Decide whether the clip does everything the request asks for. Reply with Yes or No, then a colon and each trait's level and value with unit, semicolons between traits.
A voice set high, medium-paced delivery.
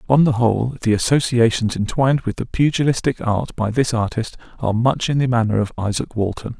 No: low, 120 Hz; average, 190 wpm